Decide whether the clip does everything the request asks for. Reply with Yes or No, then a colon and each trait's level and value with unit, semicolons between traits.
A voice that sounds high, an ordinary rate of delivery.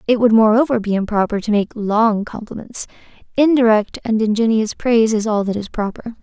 Yes: high, 220 Hz; average, 175 wpm